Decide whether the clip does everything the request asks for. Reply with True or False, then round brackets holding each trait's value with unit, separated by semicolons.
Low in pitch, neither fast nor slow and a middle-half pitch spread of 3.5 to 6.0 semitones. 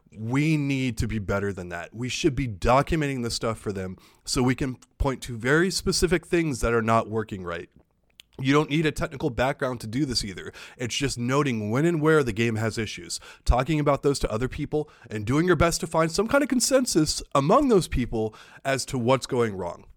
False (130 Hz; 215 wpm; 5.3 semitones)